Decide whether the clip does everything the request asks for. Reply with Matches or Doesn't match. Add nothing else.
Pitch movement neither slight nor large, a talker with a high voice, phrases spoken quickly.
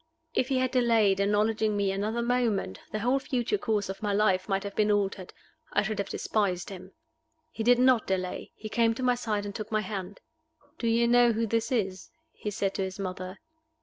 Matches